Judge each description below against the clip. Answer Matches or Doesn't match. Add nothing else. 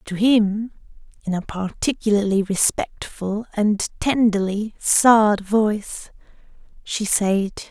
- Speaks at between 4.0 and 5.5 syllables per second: Doesn't match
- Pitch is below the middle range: Doesn't match